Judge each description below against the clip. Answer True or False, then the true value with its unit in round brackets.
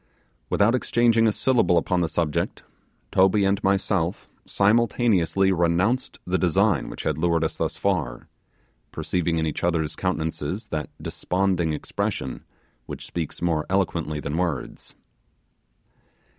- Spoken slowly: True (125 wpm)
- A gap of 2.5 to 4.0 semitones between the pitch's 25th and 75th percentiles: True (3.4 semitones)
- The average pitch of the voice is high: False (90 Hz)